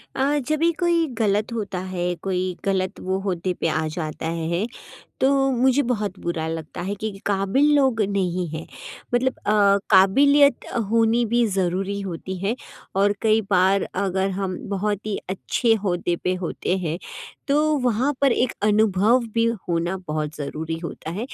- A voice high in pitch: Yes, high, 195 Hz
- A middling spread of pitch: Yes, average, 4.3 semitones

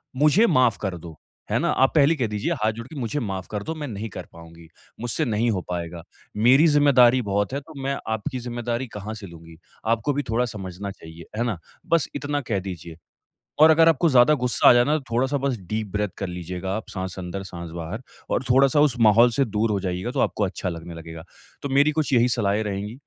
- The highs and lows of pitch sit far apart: Yes, wide, 6.1 semitones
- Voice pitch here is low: Yes, low, 110 Hz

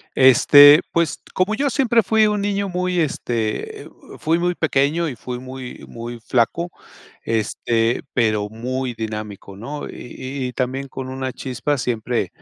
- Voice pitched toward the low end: Yes, low, 130 Hz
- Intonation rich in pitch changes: Yes, wide, 6.2 semitones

